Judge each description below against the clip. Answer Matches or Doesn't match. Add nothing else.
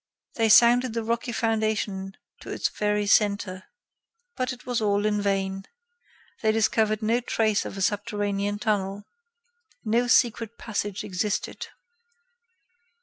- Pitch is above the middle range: Matches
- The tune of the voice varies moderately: Doesn't match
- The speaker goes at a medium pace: Doesn't match